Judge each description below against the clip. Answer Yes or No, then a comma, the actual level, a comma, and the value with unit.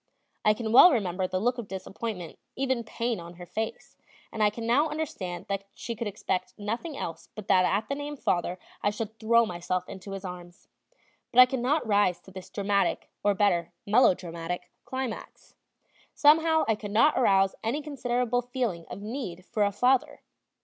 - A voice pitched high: Yes, high, 215 Hz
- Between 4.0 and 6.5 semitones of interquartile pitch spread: Yes, average, 4.9 semitones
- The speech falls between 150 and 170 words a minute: No, average, 180 wpm